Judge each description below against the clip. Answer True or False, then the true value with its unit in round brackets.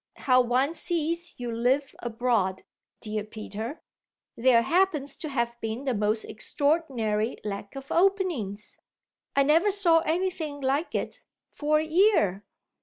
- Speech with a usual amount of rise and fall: False (6.4 semitones)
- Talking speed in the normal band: False (130 wpm)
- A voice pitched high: True (270 Hz)